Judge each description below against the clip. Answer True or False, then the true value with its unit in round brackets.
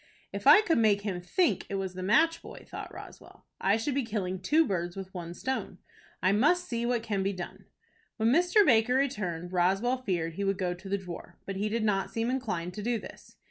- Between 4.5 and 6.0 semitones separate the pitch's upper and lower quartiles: True (4.9 semitones)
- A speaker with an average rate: False (220 wpm)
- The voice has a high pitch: True (205 Hz)